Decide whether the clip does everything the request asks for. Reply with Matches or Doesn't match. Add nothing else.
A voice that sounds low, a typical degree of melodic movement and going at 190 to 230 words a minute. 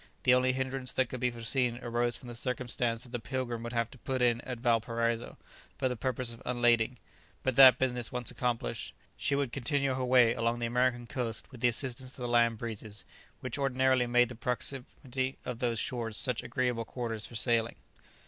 Doesn't match